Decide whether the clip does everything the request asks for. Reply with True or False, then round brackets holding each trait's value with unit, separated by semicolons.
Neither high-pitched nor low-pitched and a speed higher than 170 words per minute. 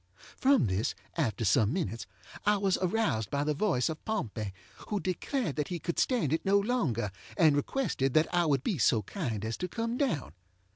True (160 Hz; 190 wpm)